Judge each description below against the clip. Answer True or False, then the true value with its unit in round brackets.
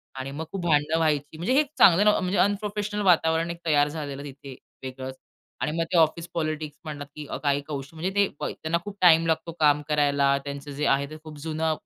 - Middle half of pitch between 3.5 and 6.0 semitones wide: False (2.7 semitones)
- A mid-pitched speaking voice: True (155 Hz)